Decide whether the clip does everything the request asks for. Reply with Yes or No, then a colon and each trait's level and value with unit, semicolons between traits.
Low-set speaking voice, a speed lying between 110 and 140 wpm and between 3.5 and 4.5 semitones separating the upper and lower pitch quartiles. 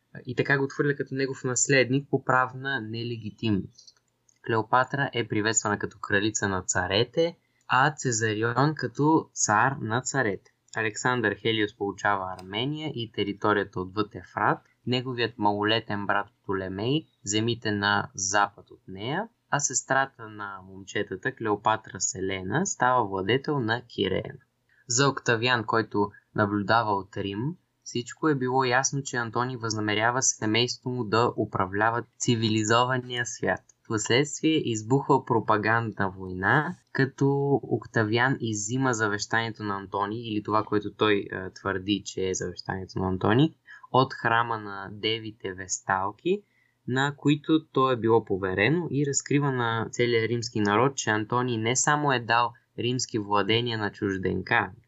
Yes: low, 115 Hz; average, 130 wpm; average, 4.1 semitones